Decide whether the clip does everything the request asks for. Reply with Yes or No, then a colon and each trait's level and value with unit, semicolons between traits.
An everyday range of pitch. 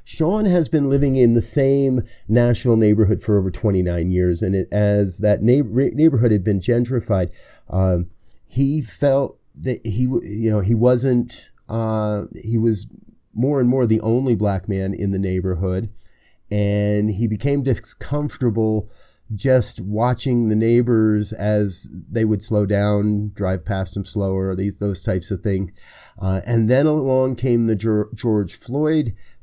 Yes: average, 3.4 semitones